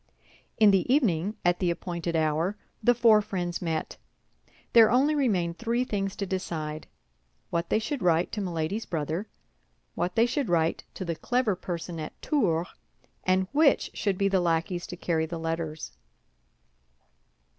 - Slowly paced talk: No, average, 150 wpm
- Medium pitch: Yes, medium, 180 Hz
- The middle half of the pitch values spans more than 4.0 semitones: Yes, average, 4.6 semitones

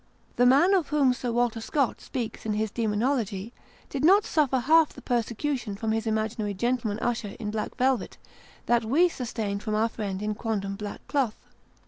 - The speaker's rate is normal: Yes, average, 175 wpm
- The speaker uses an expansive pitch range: No, average, 3.7 semitones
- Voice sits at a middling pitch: No, high, 230 Hz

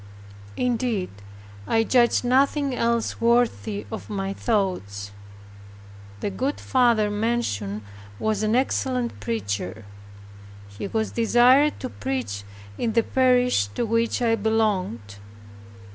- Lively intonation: No, average, 4.4 semitones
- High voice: Yes, high, 225 Hz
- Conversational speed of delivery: No, slow, 110 wpm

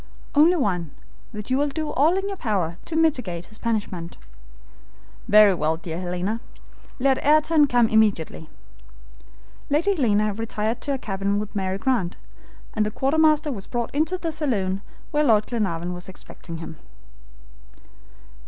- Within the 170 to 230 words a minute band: No, average, 145 wpm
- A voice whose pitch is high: Yes, high, 220 Hz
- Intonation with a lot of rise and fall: Yes, wide, 7.5 semitones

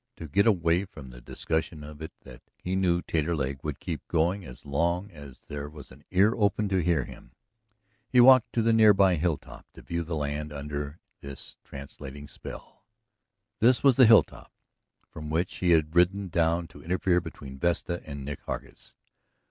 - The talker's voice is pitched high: No, very low, 85 Hz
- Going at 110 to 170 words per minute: No, average, 180 wpm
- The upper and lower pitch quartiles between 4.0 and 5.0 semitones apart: Yes, average, 4.3 semitones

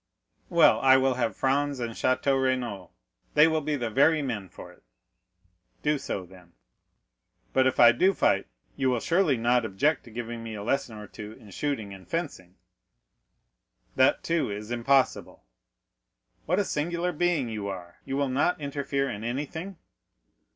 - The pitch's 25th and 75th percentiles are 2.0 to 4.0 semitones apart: No, average, 4.7 semitones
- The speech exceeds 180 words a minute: No, average, 160 wpm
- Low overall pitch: Yes, low, 130 Hz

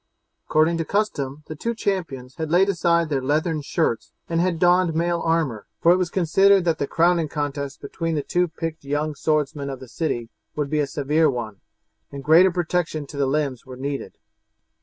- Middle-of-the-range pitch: Yes, medium, 155 Hz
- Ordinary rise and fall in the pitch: Yes, average, 3.4 semitones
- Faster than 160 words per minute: Yes, average, 190 wpm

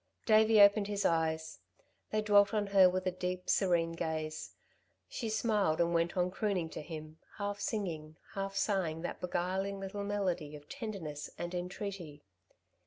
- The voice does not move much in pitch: No, average, 3.5 semitones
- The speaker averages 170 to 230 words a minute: No, average, 155 wpm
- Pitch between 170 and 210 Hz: Yes, medium, 185 Hz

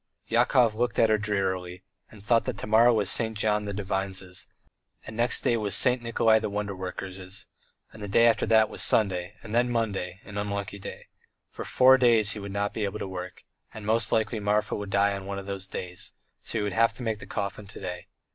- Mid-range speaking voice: No, low, 105 Hz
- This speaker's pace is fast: Yes, fast, 220 wpm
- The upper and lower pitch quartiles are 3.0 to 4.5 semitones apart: No, narrow, 2.5 semitones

